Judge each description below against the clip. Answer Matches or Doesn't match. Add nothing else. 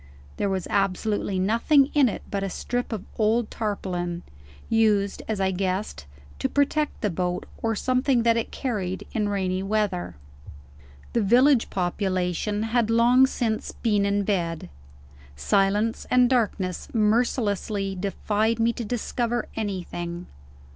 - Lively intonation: Doesn't match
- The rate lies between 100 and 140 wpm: Matches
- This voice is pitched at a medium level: Doesn't match